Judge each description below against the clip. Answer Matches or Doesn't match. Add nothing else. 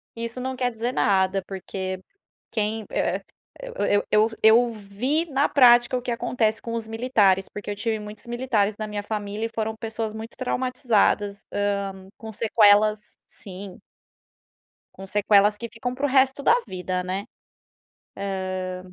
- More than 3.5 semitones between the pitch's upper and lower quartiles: Doesn't match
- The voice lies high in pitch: Matches